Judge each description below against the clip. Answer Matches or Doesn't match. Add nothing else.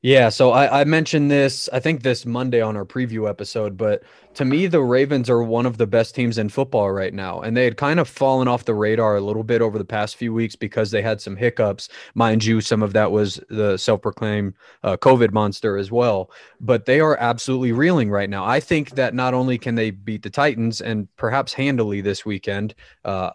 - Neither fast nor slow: Doesn't match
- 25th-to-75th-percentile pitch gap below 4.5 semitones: Matches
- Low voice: Matches